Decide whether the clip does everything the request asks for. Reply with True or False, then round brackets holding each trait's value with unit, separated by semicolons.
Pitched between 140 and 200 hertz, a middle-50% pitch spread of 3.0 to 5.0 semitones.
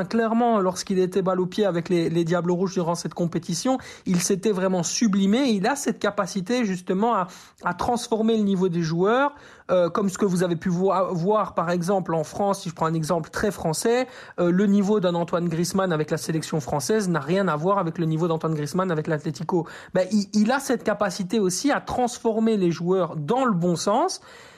True (190 Hz; 3.8 semitones)